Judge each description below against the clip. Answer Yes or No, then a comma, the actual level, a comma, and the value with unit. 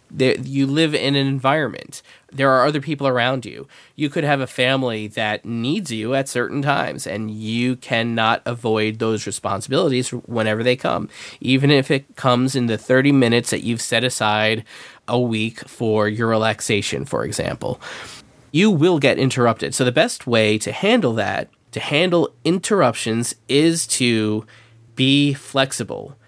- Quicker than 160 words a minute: No, average, 155 wpm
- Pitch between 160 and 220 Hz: No, low, 125 Hz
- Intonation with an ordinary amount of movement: Yes, average, 3.5 semitones